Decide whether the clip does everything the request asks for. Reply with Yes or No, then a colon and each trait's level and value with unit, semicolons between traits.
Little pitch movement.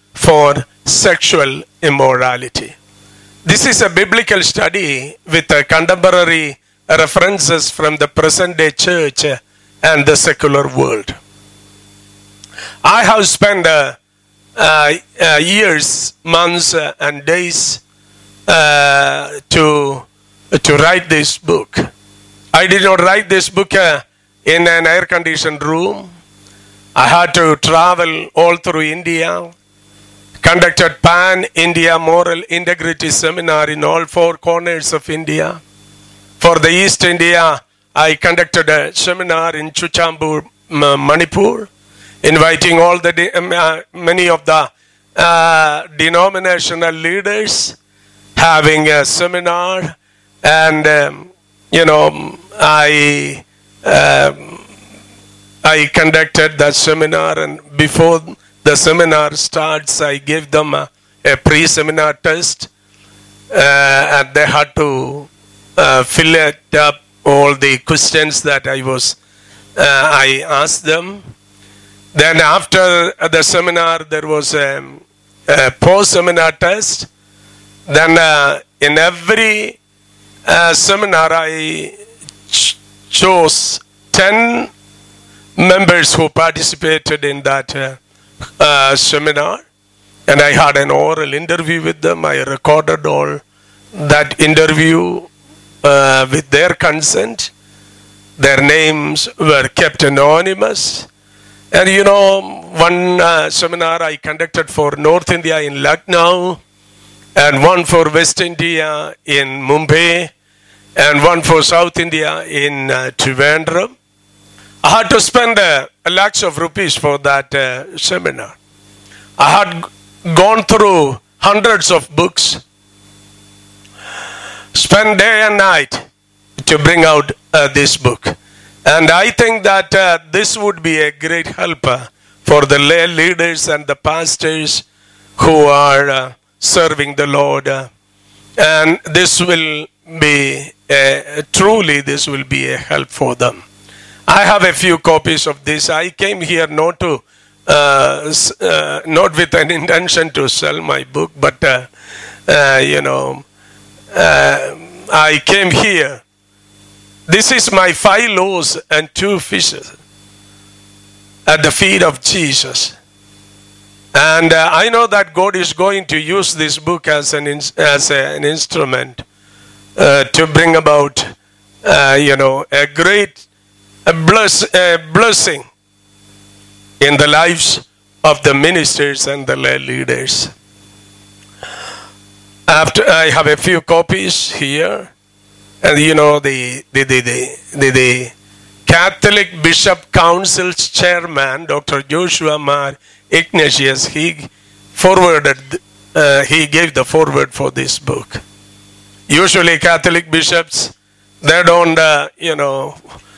No: average, 5.3 semitones